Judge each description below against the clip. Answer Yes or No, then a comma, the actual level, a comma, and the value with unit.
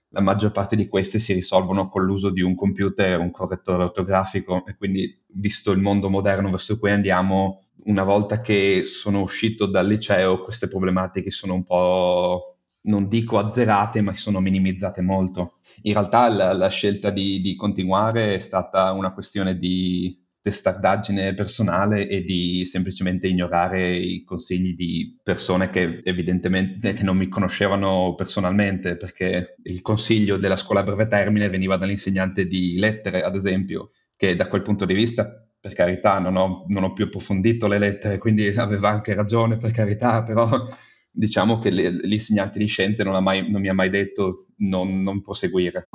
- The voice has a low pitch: Yes, very low, 95 Hz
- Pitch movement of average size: No, narrow, 1.8 semitones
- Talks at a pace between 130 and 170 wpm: Yes, average, 165 wpm